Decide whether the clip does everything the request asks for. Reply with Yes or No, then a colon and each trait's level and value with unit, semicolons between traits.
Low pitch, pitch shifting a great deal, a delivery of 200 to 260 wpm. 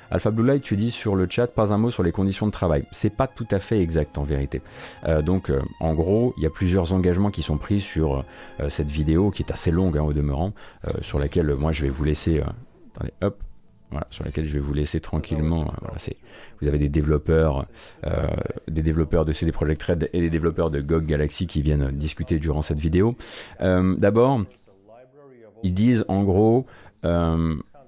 No: very low, 85 Hz; average, 4.7 semitones; average, 215 wpm